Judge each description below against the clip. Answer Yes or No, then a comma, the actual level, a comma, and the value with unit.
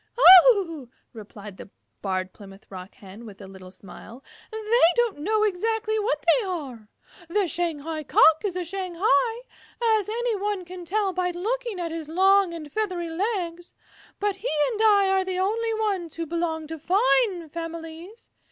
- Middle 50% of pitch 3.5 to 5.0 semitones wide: Yes, average, 4.7 semitones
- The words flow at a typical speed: Yes, average, 160 wpm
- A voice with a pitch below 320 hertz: No, very high, 360 Hz